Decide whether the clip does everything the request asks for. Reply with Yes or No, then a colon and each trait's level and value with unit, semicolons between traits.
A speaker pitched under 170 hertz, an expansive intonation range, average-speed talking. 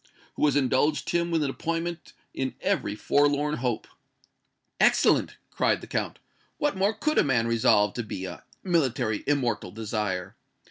Yes: low, 135 Hz; wide, 6.9 semitones; average, 150 wpm